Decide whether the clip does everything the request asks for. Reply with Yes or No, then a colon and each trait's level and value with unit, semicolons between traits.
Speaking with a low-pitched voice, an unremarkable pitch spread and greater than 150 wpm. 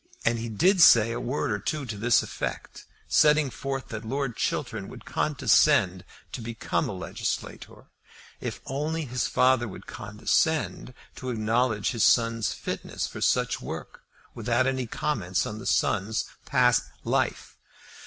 No: low, 120 Hz; average, 3.3 semitones; average, 145 wpm